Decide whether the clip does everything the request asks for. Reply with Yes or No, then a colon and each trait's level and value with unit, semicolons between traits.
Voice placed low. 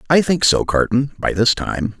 Yes: low, 120 Hz